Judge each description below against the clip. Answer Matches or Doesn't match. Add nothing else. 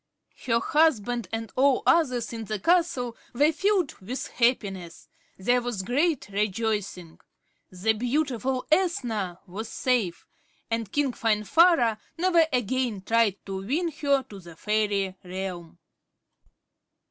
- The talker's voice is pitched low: Doesn't match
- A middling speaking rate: Doesn't match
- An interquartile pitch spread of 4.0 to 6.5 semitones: Matches